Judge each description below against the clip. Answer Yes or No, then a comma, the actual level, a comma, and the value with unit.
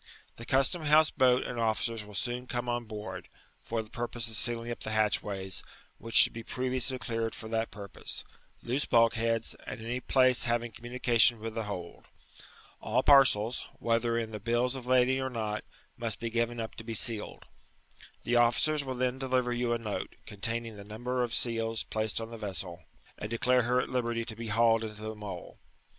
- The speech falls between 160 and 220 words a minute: Yes, average, 190 wpm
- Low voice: Yes, low, 115 Hz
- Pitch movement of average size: No, narrow, 2.0 semitones